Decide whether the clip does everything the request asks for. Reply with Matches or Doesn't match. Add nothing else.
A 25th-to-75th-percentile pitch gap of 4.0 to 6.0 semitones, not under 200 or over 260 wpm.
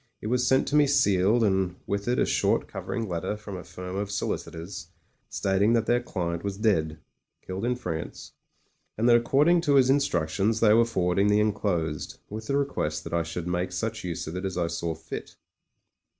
Matches